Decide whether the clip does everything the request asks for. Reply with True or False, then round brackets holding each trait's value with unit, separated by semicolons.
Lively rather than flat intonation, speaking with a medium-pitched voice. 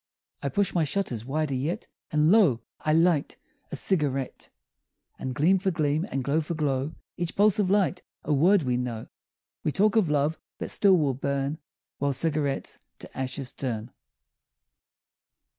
False (4.5 semitones; 150 Hz)